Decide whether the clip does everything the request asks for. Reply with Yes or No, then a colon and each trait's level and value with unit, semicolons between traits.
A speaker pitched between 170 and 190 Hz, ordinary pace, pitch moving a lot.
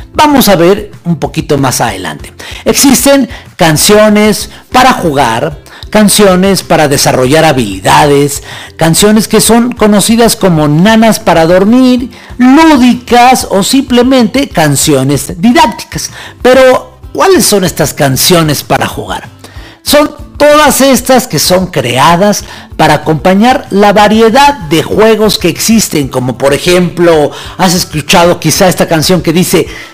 No: medium, 185 Hz; slow, 120 wpm; wide, 7.4 semitones